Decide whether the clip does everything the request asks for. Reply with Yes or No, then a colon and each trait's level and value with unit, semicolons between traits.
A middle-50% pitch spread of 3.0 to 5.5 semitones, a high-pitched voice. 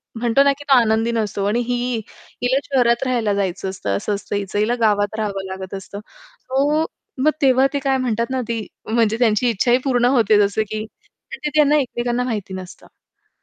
Yes: average, 3.6 semitones; high, 230 Hz